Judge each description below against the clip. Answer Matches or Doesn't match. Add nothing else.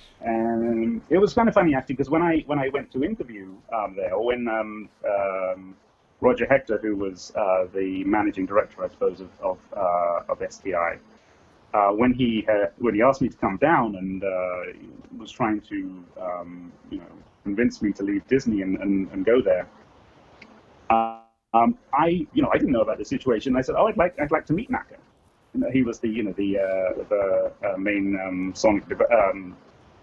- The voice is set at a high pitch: Doesn't match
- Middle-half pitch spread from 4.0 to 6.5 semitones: Matches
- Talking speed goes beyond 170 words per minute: Matches